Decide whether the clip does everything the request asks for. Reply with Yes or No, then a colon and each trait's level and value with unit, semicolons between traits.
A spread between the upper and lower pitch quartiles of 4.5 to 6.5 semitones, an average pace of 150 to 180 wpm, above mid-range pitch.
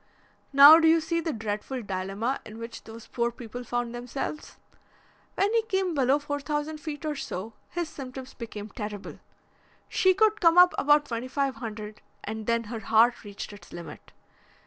Yes: wide, 5.5 semitones; average, 170 wpm; very high, 250 Hz